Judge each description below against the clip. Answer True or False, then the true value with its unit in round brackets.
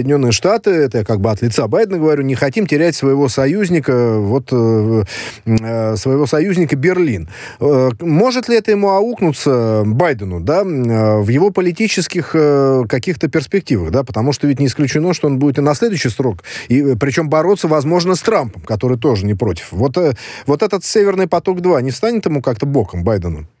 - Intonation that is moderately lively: False (6.4 semitones)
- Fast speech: True (180 wpm)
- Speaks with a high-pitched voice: False (140 Hz)